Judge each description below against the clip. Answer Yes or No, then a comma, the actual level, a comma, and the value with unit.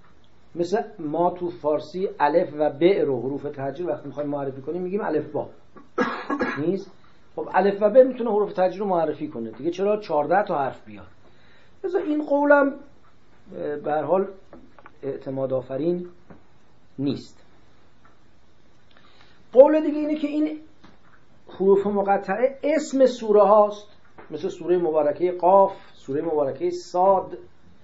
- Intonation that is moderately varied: No, wide, 6.8 semitones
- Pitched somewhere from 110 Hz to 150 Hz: No, medium, 185 Hz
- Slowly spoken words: Yes, slow, 125 wpm